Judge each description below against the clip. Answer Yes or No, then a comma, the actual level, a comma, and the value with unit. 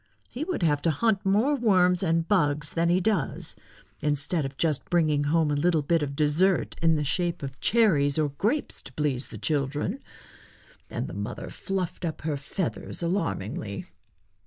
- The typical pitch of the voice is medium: Yes, medium, 165 Hz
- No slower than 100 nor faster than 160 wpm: No, average, 170 wpm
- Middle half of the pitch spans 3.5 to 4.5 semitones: Yes, average, 4.2 semitones